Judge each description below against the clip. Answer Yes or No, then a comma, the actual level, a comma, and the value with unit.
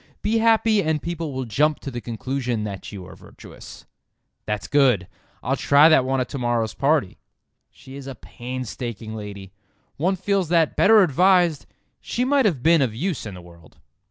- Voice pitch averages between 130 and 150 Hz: Yes, low, 135 Hz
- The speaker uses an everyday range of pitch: No, wide, 6.8 semitones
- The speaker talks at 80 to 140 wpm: No, average, 180 wpm